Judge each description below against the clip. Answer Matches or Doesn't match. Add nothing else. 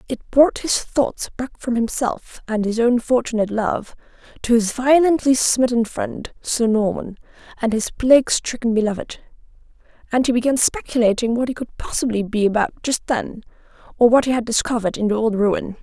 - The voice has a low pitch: Doesn't match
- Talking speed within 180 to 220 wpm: Doesn't match